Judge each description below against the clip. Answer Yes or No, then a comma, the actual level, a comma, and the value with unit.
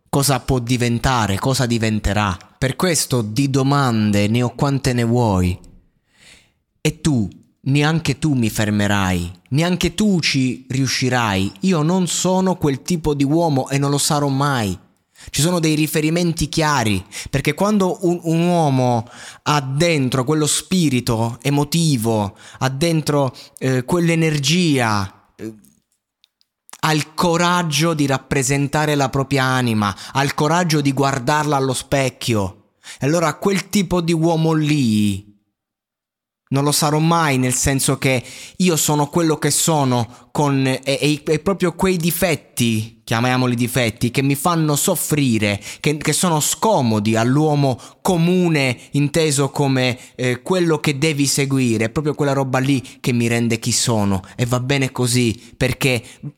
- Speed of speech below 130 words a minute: No, average, 140 wpm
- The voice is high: No, medium, 140 Hz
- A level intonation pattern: No, average, 4.3 semitones